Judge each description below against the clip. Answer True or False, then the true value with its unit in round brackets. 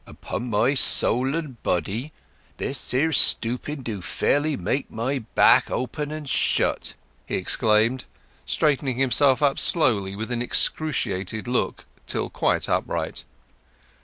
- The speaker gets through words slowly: True (120 wpm)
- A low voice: True (125 Hz)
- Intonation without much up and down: False (4.4 semitones)